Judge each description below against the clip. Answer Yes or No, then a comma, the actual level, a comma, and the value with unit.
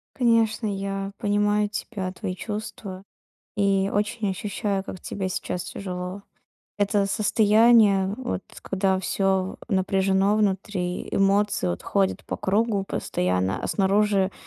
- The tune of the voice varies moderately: No, narrow, 1.7 semitones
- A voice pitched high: Yes, high, 195 Hz